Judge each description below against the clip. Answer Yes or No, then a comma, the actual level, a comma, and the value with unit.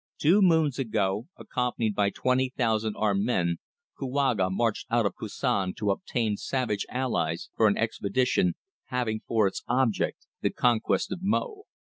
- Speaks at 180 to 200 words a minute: No, average, 145 wpm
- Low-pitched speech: Yes, low, 115 Hz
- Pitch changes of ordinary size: Yes, average, 4.1 semitones